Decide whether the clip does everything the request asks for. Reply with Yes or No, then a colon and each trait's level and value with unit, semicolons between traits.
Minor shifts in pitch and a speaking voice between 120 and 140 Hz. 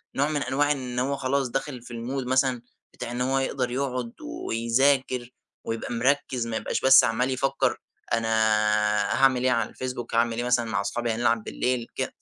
Yes: narrow, 2.2 semitones; low, 125 Hz